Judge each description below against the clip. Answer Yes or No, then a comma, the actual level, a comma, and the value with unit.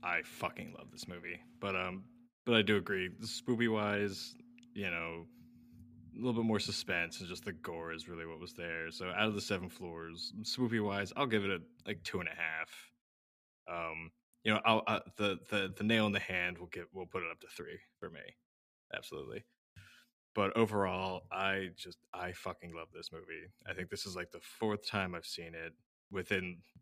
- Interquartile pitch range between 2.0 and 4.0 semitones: No, average, 4.4 semitones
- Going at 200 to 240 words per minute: Yes, fast, 205 wpm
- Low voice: Yes, very low, 95 Hz